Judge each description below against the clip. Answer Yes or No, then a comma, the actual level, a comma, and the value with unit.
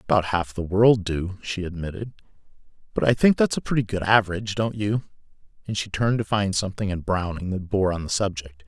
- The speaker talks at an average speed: No, fast, 210 wpm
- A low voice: Yes, low, 100 Hz